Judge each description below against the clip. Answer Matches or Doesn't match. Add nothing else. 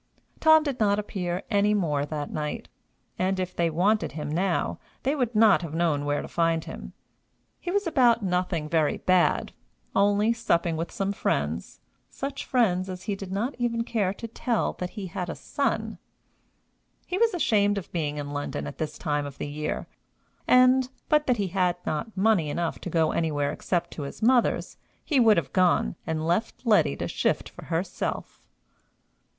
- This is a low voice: Doesn't match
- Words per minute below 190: Matches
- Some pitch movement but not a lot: Doesn't match